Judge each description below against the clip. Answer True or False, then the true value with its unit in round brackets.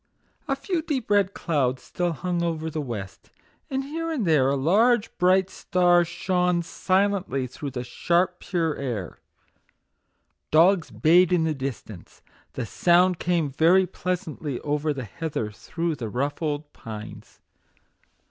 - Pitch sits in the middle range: True (165 Hz)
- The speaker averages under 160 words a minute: True (145 wpm)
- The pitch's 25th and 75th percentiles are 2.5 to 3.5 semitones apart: False (4.8 semitones)